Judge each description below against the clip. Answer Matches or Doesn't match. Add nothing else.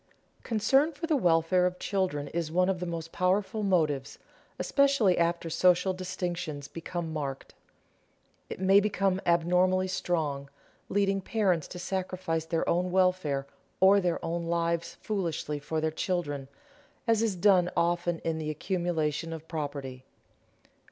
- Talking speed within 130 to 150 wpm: Matches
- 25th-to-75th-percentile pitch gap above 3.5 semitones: Doesn't match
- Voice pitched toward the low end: Doesn't match